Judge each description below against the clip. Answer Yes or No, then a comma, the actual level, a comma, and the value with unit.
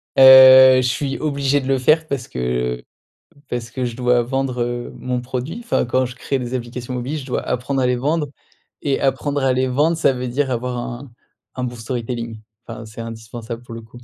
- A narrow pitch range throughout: Yes, narrow, 2.0 semitones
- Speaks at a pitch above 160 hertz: No, low, 125 Hz